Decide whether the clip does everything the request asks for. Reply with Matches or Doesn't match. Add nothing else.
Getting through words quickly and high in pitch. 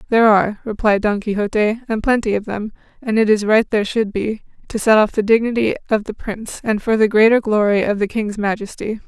Matches